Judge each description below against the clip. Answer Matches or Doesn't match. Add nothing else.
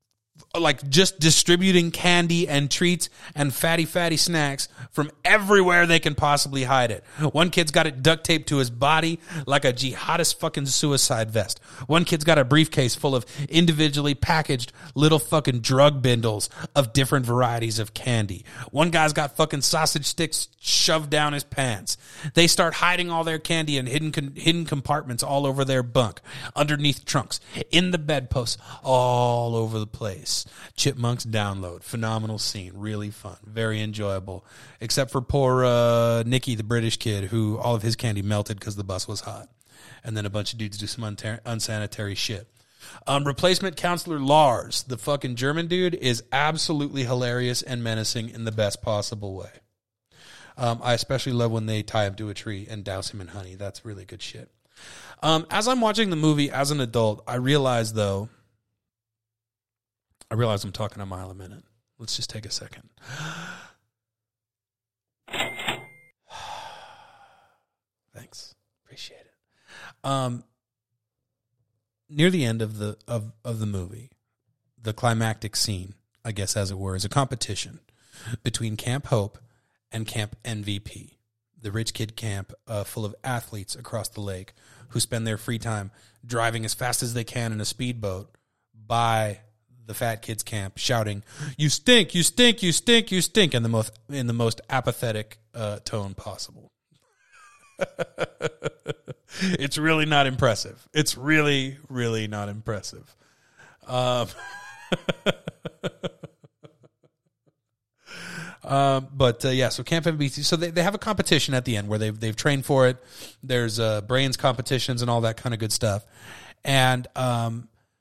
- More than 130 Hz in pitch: Doesn't match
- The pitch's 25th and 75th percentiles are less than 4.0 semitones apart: Doesn't match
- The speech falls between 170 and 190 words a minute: Doesn't match